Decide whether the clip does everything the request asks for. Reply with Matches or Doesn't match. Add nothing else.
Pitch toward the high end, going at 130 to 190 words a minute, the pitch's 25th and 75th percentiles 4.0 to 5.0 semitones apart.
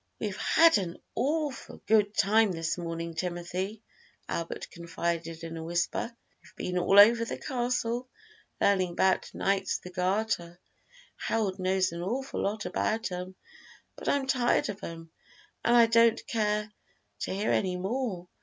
Matches